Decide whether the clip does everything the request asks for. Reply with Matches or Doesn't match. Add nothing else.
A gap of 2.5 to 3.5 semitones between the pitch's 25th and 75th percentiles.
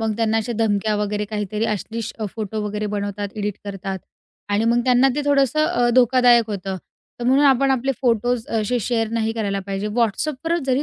Matches